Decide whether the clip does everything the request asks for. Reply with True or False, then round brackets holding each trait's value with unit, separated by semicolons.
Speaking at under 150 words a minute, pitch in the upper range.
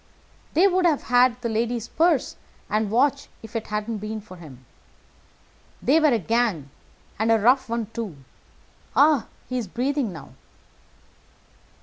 True (140 wpm; 230 Hz)